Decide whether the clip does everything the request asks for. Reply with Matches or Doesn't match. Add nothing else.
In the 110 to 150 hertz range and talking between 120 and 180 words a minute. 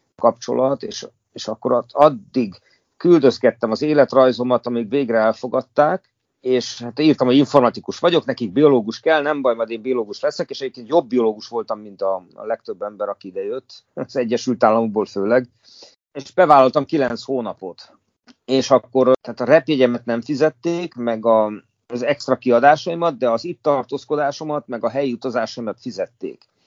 Matches